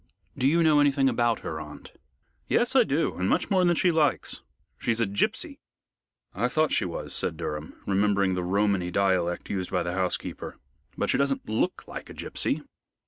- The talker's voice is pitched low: Yes, low, 105 Hz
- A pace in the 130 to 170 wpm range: No, average, 185 wpm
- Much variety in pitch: Yes, wide, 7.8 semitones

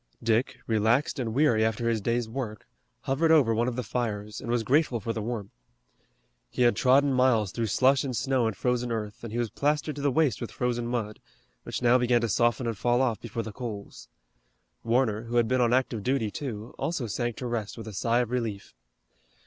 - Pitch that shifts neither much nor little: No, narrow, 2.3 semitones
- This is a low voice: Yes, low, 120 Hz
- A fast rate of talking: Yes, fast, 215 wpm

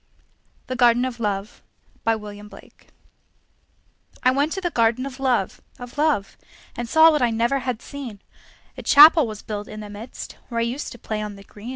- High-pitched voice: Yes, high, 235 Hz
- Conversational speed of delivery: Yes, average, 170 wpm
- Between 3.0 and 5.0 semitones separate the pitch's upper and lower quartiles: Yes, average, 3.8 semitones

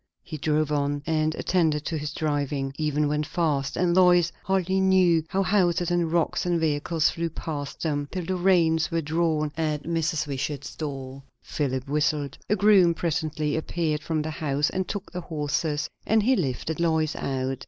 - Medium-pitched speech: Yes, medium, 155 Hz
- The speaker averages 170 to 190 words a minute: Yes, average, 175 wpm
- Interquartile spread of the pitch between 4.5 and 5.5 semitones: No, average, 2.8 semitones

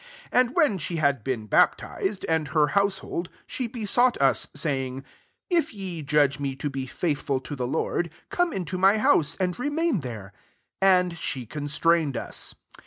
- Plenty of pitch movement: Yes, wide, 6.0 semitones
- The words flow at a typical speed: Yes, average, 170 wpm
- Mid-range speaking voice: Yes, medium, 160 Hz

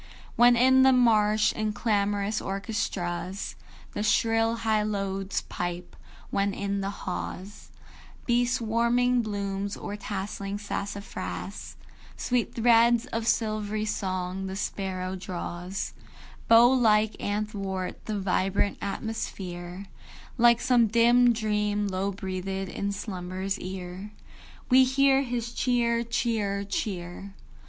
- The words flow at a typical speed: No, slow, 110 wpm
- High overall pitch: Yes, high, 205 Hz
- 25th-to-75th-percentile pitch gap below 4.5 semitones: Yes, average, 3.2 semitones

